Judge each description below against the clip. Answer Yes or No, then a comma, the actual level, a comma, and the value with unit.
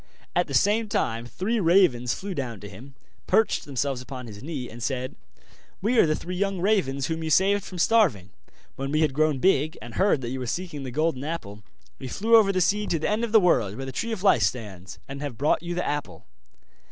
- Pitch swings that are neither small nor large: No, wide, 7.2 semitones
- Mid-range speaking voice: Yes, medium, 150 Hz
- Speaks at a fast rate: Yes, fast, 230 wpm